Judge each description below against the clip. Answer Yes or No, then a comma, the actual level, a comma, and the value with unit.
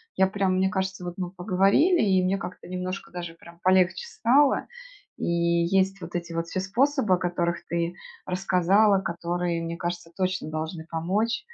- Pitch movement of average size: No, narrow, 2.2 semitones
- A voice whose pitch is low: No, medium, 185 Hz